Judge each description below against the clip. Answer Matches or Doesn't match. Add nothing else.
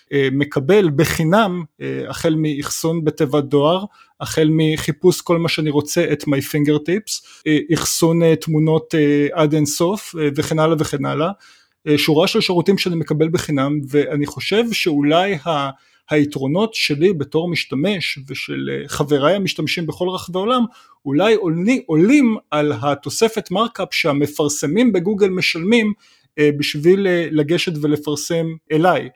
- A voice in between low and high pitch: Matches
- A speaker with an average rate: Matches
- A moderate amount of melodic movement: Matches